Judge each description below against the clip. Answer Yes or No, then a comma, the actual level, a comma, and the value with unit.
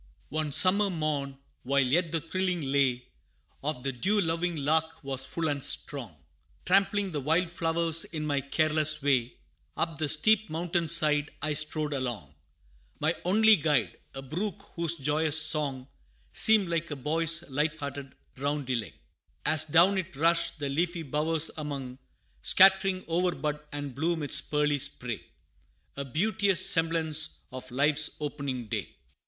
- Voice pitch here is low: No, medium, 155 Hz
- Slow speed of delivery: No, average, 145 wpm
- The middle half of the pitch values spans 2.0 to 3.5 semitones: Yes, average, 3.1 semitones